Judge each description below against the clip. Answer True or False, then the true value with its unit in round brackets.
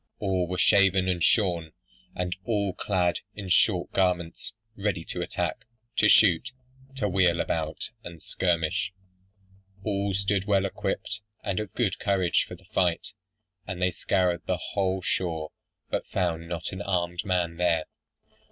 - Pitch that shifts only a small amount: True (2.2 semitones)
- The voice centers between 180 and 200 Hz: False (90 Hz)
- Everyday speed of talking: True (145 wpm)